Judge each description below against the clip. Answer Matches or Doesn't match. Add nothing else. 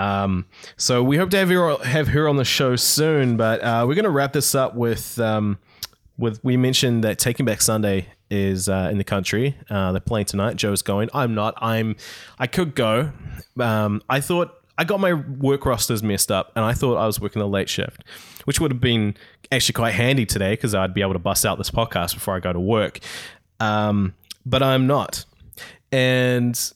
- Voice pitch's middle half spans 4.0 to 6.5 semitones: Matches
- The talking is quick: Matches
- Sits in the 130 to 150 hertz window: Doesn't match